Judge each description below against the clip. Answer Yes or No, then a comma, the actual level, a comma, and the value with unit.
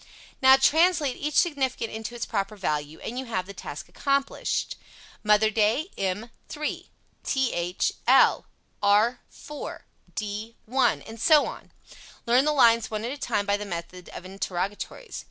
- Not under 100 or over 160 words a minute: Yes, average, 155 wpm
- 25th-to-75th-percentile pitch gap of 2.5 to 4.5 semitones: No, average, 4.9 semitones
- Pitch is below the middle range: No, high, 225 Hz